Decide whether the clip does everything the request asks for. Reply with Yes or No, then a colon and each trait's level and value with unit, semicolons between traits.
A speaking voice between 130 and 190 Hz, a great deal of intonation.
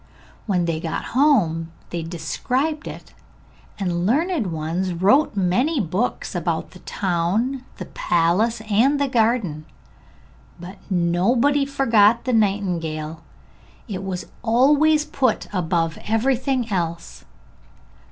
No: high, 205 Hz; wide, 6.9 semitones